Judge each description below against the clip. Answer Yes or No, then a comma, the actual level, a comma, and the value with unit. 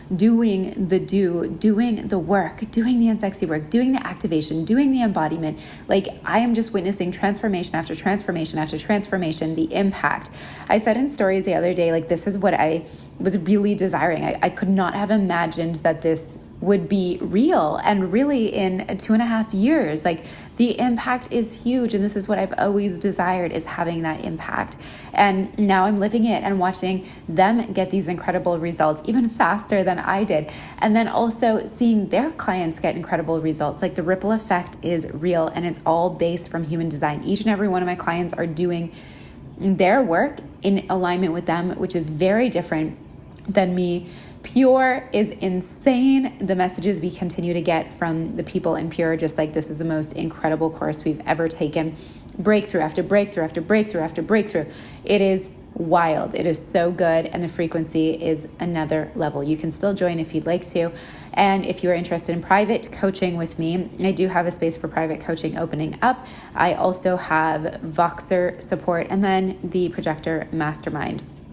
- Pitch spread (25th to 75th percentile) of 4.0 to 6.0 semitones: No, average, 3.5 semitones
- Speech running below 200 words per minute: Yes, average, 185 wpm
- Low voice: No, medium, 180 Hz